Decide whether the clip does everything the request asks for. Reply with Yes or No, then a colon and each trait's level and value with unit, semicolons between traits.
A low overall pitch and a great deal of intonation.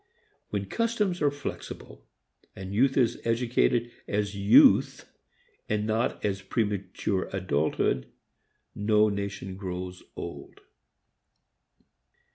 No: low, 105 Hz; average, 3.5 semitones